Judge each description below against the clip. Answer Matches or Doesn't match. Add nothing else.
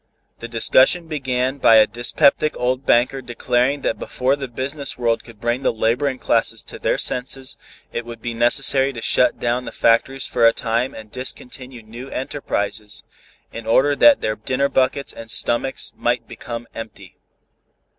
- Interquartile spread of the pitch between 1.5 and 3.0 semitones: Matches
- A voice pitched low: Matches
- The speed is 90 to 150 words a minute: Doesn't match